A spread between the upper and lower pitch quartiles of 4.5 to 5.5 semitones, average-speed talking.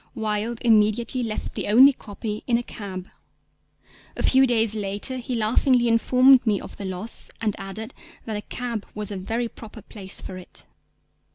No: narrow, 2.5 semitones; average, 170 wpm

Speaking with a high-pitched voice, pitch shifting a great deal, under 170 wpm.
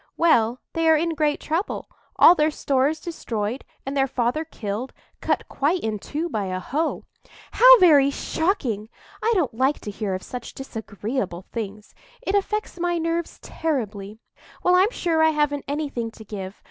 Yes: very high, 280 Hz; wide, 6.8 semitones; average, 160 wpm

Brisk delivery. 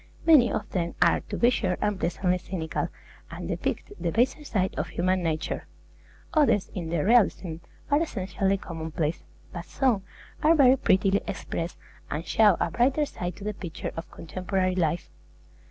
No: average, 155 wpm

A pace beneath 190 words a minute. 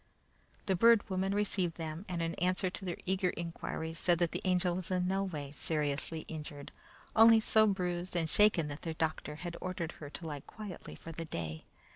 No: average, 195 wpm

